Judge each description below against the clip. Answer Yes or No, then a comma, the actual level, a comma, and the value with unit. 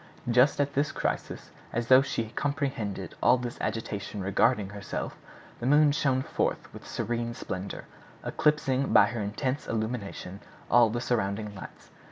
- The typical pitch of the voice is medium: No, low, 120 Hz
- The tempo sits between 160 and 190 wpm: No, average, 145 wpm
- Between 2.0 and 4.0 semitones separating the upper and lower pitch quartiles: No, average, 4.4 semitones